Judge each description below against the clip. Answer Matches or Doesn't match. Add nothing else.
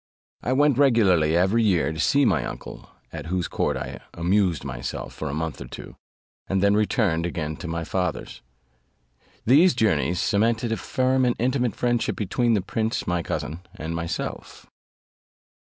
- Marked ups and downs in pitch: Matches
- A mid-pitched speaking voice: Doesn't match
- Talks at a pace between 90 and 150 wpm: Doesn't match